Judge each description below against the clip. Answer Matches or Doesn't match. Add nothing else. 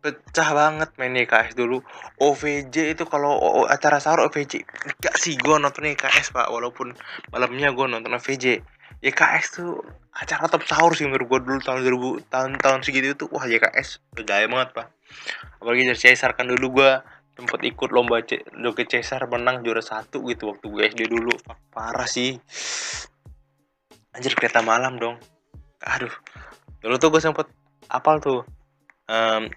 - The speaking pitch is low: Matches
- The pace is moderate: Doesn't match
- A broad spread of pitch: Doesn't match